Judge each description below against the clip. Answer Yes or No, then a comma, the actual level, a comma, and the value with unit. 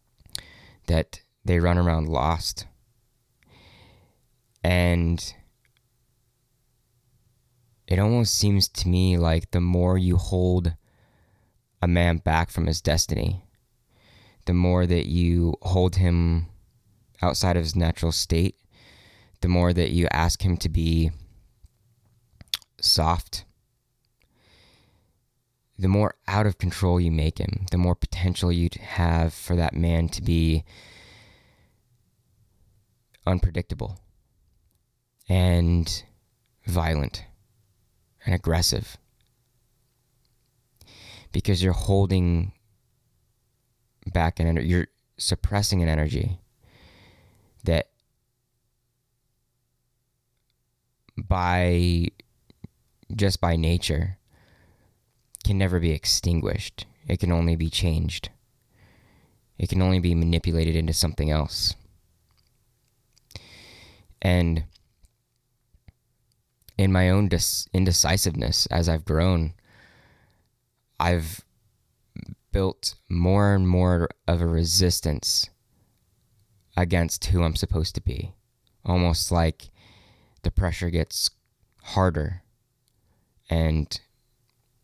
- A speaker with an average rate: No, slow, 90 wpm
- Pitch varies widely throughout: No, average, 5.0 semitones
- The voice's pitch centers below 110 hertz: Yes, very low, 95 Hz